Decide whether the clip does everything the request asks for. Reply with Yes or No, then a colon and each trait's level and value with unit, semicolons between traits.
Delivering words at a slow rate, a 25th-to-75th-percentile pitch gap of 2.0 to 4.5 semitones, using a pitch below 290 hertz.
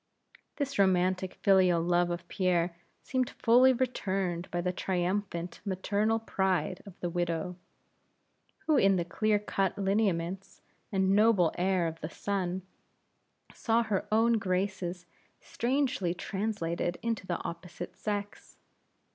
Yes: slow, 120 wpm; average, 3.0 semitones; high, 190 Hz